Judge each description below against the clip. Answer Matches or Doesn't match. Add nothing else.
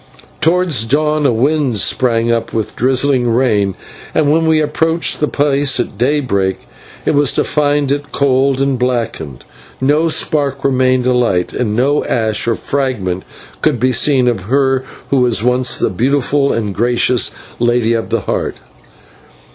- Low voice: Matches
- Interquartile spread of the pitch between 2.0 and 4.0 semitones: Matches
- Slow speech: Doesn't match